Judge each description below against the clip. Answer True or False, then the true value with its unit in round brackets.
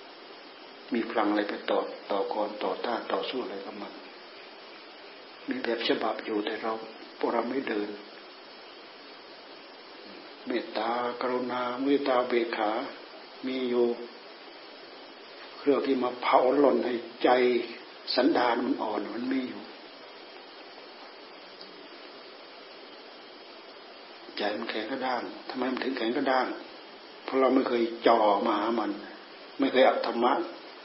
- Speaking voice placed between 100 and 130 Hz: True (125 Hz)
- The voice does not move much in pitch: True (1.4 semitones)